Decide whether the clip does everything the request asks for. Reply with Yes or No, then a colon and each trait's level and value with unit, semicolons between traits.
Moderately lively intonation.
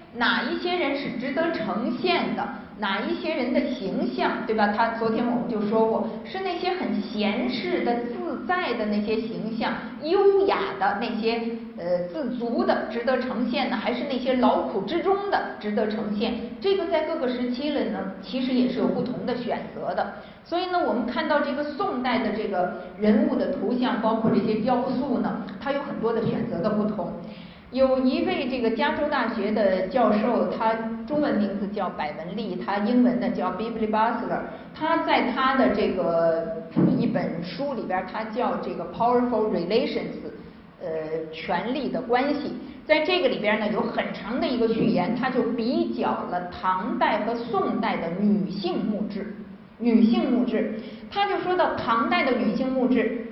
Yes: average, 3.7 semitones